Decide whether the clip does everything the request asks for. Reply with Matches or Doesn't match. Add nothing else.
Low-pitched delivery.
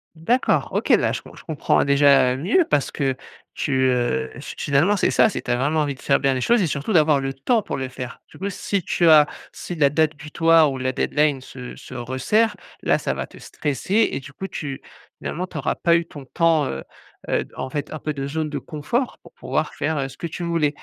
Doesn't match